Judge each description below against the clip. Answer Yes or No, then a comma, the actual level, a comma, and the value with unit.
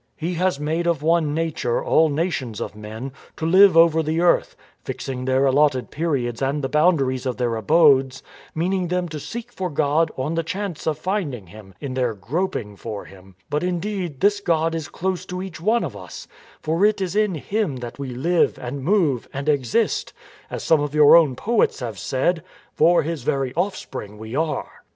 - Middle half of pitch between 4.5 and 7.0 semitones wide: Yes, average, 5.1 semitones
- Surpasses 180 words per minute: Yes, average, 195 wpm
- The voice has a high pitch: No, medium, 155 Hz